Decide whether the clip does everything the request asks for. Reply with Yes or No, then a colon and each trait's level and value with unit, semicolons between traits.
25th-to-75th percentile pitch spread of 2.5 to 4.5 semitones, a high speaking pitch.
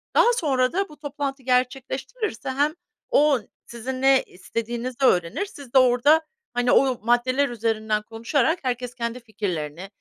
Yes: average, 3.1 semitones; very high, 255 Hz